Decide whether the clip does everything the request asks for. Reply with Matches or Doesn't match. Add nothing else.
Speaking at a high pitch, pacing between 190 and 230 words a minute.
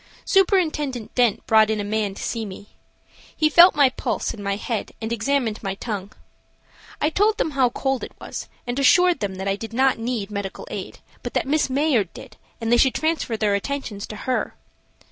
Matches